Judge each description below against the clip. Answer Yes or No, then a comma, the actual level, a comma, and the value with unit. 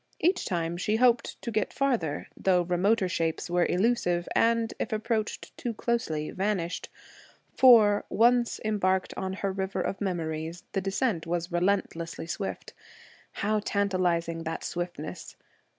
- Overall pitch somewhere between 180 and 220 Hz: Yes, high, 190 Hz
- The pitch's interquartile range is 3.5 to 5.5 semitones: Yes, average, 3.9 semitones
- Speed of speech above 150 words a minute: No, slow, 135 wpm